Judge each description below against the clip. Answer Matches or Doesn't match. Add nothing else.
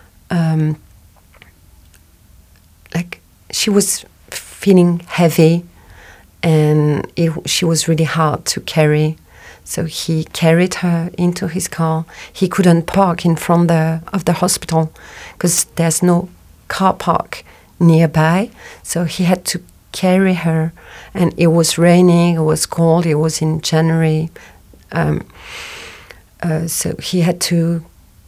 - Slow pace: Matches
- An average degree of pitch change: Doesn't match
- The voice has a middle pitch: Matches